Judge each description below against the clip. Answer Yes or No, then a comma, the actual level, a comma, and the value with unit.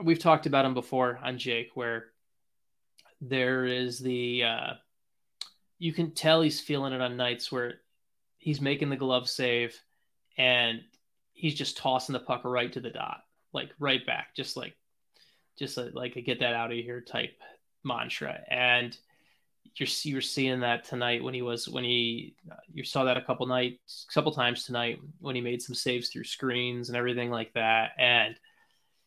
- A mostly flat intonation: Yes, narrow, 1.9 semitones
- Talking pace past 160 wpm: Yes, average, 175 wpm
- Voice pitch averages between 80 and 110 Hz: No, low, 125 Hz